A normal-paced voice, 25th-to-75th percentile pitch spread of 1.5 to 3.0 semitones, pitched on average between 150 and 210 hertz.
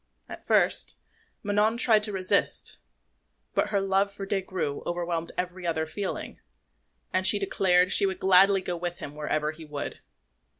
Yes: average, 160 wpm; average, 2.7 semitones; medium, 185 Hz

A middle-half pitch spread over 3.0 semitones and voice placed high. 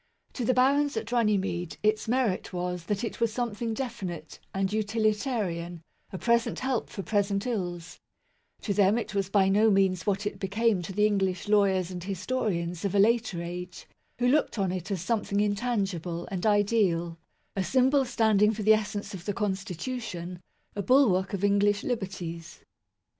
Yes: average, 3.4 semitones; high, 205 Hz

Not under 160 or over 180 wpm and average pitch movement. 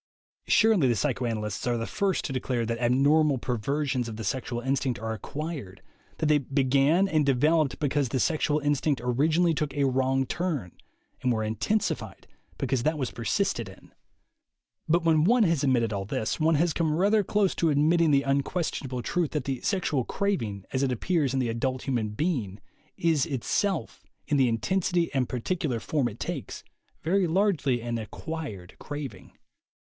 Yes: average, 170 wpm; average, 5.0 semitones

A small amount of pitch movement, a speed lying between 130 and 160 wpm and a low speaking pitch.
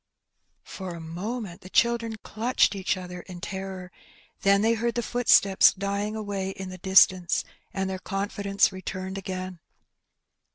No: narrow, 1.9 semitones; average, 150 wpm; high, 195 Hz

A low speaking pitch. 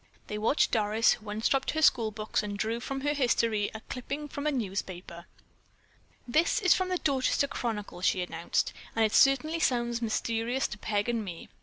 No: high, 230 Hz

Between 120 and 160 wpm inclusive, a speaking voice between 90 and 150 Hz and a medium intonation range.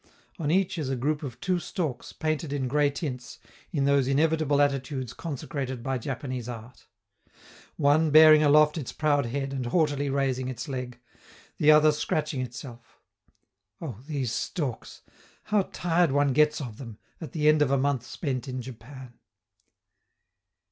Yes: average, 155 wpm; medium, 140 Hz; average, 3.0 semitones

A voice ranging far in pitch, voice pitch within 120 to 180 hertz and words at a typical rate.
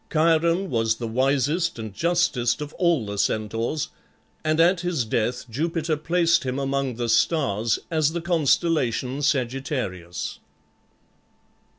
No: wide, 5.9 semitones; medium, 140 Hz; slow, 120 wpm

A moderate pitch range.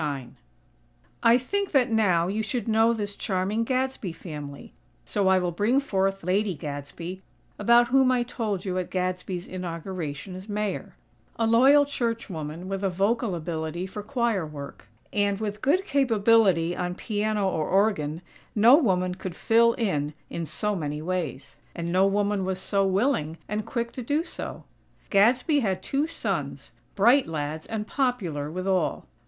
Yes: average, 4.7 semitones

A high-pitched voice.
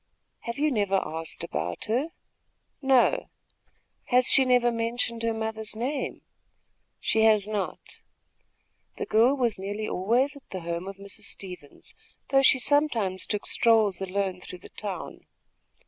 Yes: high, 220 Hz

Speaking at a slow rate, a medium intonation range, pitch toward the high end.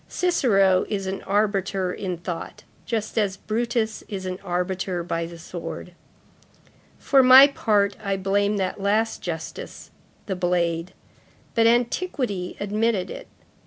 Yes: slow, 130 wpm; average, 3.5 semitones; high, 195 Hz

